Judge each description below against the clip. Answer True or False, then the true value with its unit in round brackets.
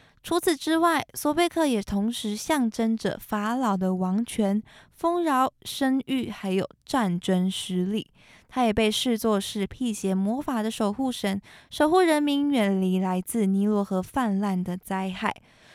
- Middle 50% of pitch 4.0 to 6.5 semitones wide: True (5.2 semitones)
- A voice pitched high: True (220 Hz)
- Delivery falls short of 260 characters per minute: True (220 characters per minute)